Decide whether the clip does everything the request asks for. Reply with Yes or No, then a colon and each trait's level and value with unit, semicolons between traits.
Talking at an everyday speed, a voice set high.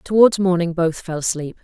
No: average, 185 wpm; medium, 175 Hz